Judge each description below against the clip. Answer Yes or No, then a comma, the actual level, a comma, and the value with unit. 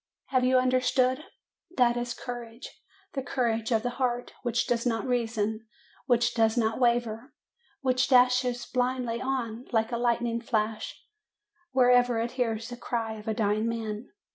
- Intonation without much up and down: Yes, narrow, 1.8 semitones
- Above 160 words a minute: No, average, 155 wpm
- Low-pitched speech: No, high, 240 Hz